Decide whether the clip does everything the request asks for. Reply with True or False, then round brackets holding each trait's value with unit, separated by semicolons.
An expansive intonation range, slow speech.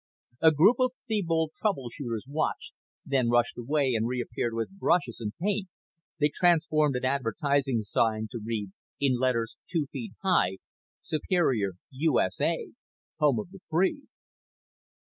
True (6.0 semitones; 130 wpm)